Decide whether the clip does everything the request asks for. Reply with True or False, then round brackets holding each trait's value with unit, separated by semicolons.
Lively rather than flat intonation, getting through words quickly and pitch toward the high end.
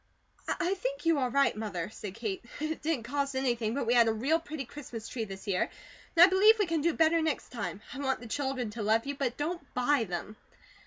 True (5.9 semitones; 230 wpm; 265 Hz)